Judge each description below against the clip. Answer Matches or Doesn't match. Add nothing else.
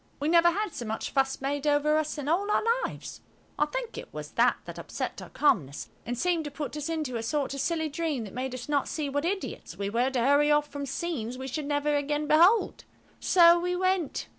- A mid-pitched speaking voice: Doesn't match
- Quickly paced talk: Matches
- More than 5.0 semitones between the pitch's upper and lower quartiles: Doesn't match